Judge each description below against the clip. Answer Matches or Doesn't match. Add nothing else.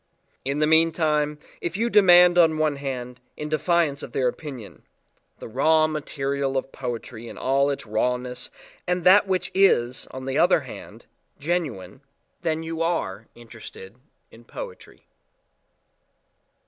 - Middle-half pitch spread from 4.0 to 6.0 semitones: Matches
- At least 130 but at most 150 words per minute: Matches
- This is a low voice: Doesn't match